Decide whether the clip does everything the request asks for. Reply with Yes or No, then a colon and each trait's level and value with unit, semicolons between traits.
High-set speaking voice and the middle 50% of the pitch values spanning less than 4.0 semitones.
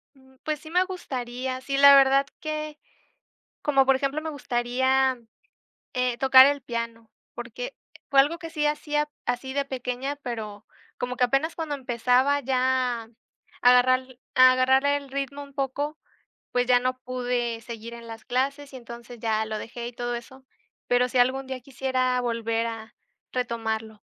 Yes: very high, 255 Hz; narrow, 2.4 semitones